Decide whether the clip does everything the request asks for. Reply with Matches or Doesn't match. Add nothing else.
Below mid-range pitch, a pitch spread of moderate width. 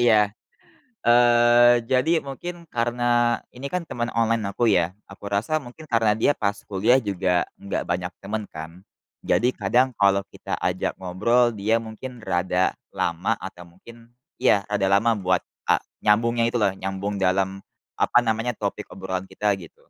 Matches